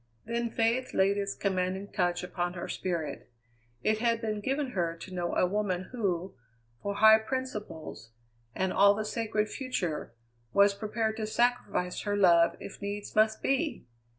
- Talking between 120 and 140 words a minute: No, average, 155 wpm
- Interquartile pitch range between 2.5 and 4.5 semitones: Yes, average, 3.4 semitones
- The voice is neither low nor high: No, high, 205 Hz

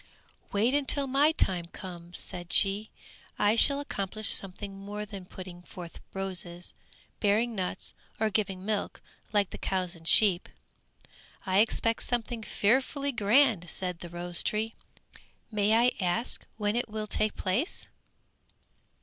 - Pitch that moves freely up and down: No, average, 3.6 semitones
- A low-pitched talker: No, high, 205 Hz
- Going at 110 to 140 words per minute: Yes, slow, 135 wpm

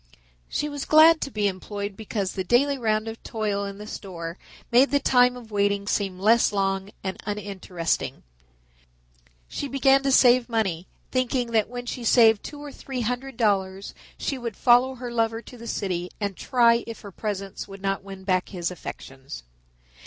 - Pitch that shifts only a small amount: No, average, 4.1 semitones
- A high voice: Yes, high, 215 Hz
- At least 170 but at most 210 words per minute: Yes, average, 180 wpm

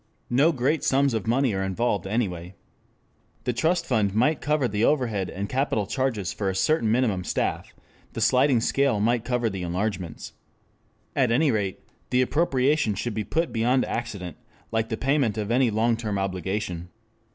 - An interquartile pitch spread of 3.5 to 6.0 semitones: Yes, average, 4.6 semitones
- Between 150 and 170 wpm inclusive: Yes, average, 165 wpm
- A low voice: Yes, low, 115 Hz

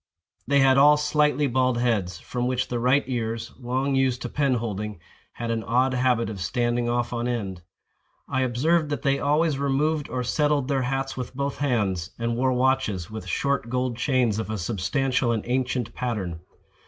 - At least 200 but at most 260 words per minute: No, average, 180 wpm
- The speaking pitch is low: Yes, low, 125 Hz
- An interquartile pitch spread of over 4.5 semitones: No, average, 2.7 semitones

